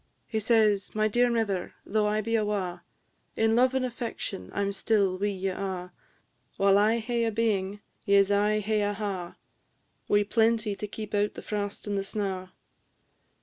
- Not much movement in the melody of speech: Yes, narrow, 2.0 semitones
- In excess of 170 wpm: Yes, average, 180 wpm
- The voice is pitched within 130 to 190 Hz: No, high, 205 Hz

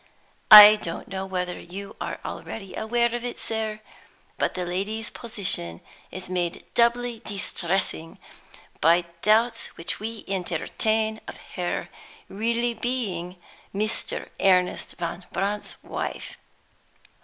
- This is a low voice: No, high, 200 Hz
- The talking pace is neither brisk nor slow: No, slow, 115 wpm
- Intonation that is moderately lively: Yes, average, 3.6 semitones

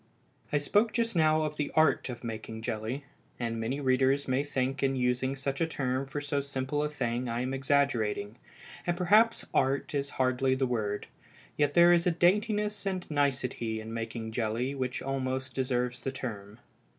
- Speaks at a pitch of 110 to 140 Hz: Yes, low, 135 Hz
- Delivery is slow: No, average, 175 wpm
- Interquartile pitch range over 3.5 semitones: No, average, 3.1 semitones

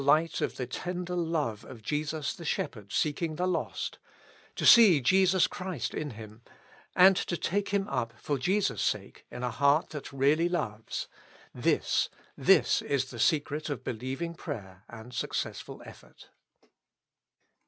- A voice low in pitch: No, medium, 150 Hz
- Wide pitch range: Yes, wide, 6.0 semitones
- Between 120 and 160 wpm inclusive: Yes, average, 150 wpm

